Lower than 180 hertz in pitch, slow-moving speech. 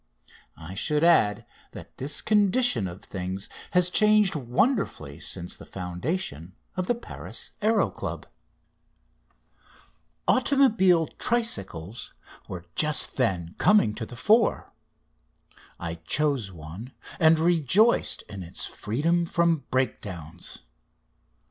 Yes: low, 135 Hz; slow, 105 wpm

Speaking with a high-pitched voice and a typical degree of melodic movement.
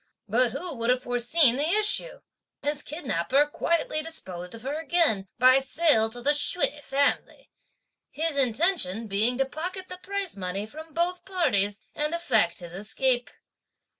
No: very high, 275 Hz; wide, 6.5 semitones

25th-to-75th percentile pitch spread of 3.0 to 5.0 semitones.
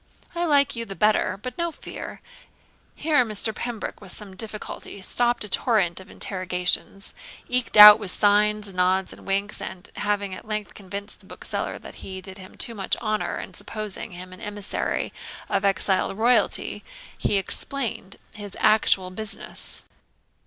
No: narrow, 2.5 semitones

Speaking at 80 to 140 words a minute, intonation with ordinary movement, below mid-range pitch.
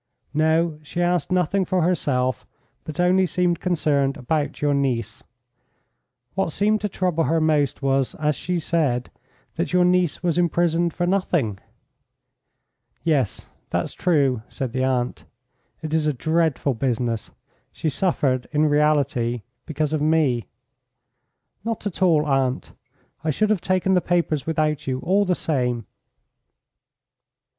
No: slow, 135 wpm; average, 4.5 semitones; medium, 155 Hz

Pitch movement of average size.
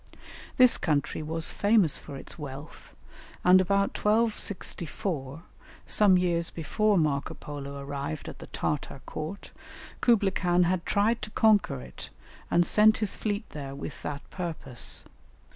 No: wide, 5.9 semitones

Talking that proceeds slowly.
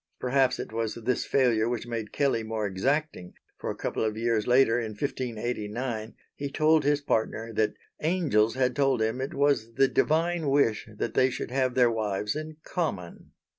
No: average, 175 wpm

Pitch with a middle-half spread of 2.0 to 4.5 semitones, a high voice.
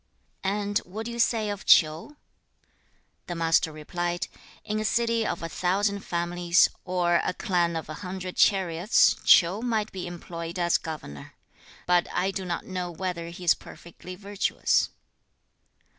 No: average, 2.9 semitones; medium, 180 Hz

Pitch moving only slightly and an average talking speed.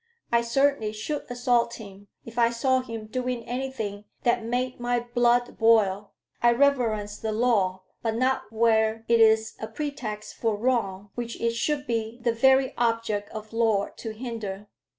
Yes: narrow, 2.1 semitones; average, 160 wpm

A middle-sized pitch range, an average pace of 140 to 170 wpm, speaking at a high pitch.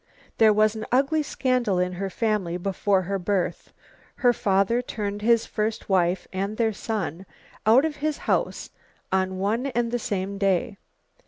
Yes: average, 3.6 semitones; average, 160 wpm; high, 210 Hz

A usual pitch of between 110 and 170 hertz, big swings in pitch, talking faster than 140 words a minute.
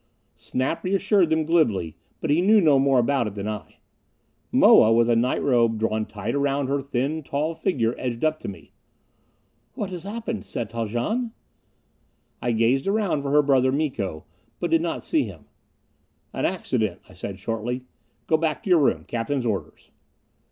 Yes: low, 135 Hz; wide, 5.7 semitones; average, 170 wpm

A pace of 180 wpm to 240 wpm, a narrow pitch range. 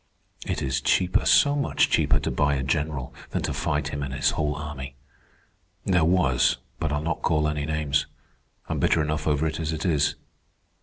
Yes: average, 185 wpm; narrow, 1.8 semitones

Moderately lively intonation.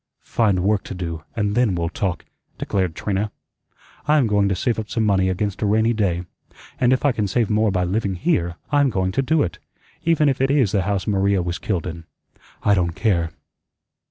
Yes: average, 3.8 semitones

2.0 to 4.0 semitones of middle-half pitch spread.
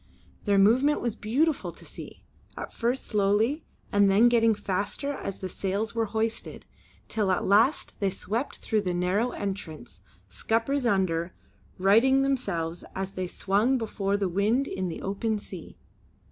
Yes: average, 3.4 semitones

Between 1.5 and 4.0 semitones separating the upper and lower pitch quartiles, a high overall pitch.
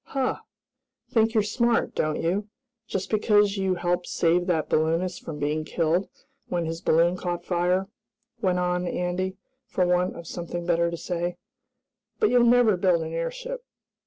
No: average, 2.8 semitones; medium, 180 Hz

